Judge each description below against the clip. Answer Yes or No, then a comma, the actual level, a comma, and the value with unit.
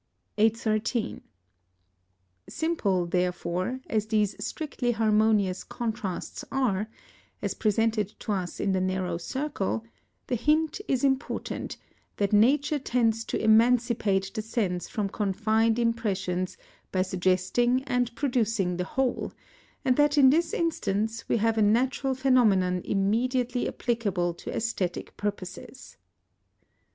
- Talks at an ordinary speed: No, slow, 115 wpm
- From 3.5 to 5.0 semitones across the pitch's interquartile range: Yes, average, 4.3 semitones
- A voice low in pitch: No, high, 220 Hz